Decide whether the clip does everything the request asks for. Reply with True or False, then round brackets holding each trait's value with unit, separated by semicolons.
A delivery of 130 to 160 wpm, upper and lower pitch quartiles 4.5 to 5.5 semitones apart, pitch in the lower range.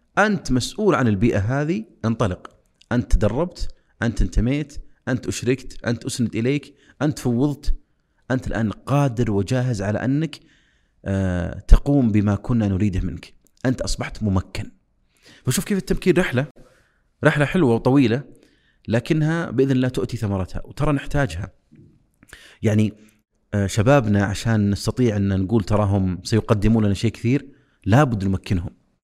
False (120 wpm; 5.1 semitones; 120 Hz)